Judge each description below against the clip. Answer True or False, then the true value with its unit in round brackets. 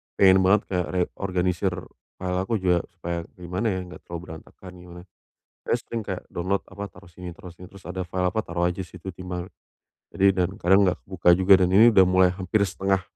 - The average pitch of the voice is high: False (90 Hz)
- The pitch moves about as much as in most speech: False (1.4 semitones)